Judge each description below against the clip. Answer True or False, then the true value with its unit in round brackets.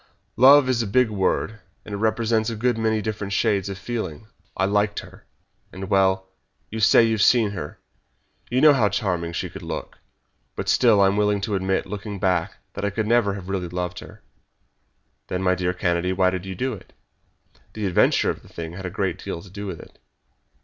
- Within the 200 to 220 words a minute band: True (205 wpm)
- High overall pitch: False (100 Hz)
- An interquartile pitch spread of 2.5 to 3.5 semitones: True (2.9 semitones)